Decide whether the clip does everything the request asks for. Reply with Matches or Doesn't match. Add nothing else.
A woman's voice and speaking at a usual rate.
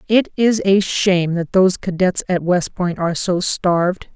Matches